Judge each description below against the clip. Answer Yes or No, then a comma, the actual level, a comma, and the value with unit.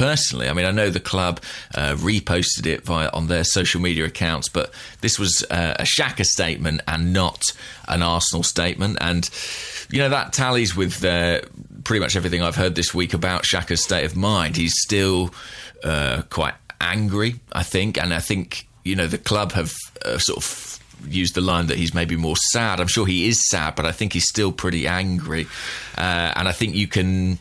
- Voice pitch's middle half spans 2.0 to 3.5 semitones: Yes, average, 2.8 semitones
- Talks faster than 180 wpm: Yes, average, 200 wpm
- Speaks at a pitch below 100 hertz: Yes, very low, 90 Hz